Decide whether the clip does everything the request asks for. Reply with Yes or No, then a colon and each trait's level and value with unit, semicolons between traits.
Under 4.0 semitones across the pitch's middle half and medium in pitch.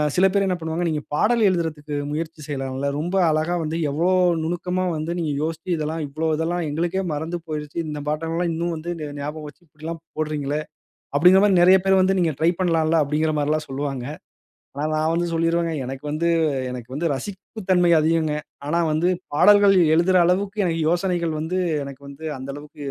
Yes: narrow, 2.6 semitones; medium, 160 Hz